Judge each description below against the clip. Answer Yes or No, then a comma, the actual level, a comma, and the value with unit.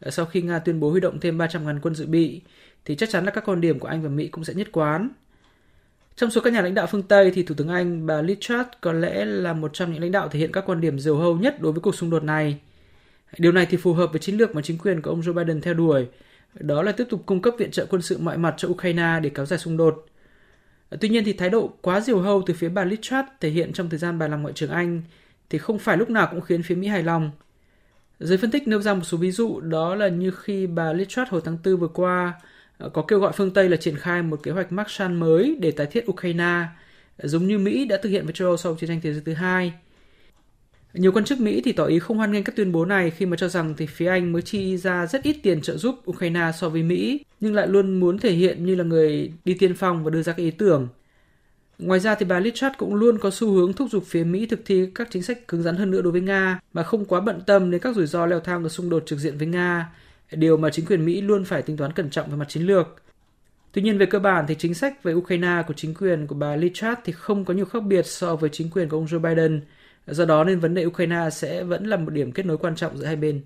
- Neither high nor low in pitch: Yes, medium, 175 Hz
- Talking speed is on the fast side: Yes, fast, 280 wpm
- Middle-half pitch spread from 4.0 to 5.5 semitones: No, average, 3.2 semitones